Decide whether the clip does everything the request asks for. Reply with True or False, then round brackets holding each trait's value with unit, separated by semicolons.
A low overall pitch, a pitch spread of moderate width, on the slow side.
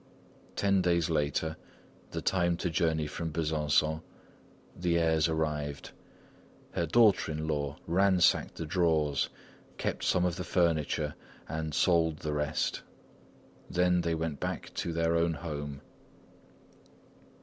False (80 Hz; 2.1 semitones; 125 wpm)